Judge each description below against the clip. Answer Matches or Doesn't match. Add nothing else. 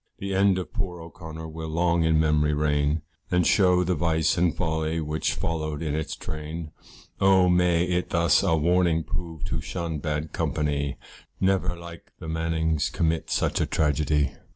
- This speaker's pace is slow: Doesn't match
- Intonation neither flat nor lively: Doesn't match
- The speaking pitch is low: Matches